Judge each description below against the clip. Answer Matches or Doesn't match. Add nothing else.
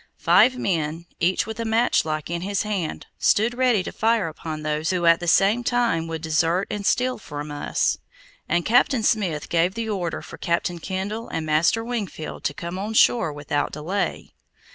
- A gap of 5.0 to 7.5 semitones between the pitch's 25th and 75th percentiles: Matches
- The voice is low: Doesn't match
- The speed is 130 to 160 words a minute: Doesn't match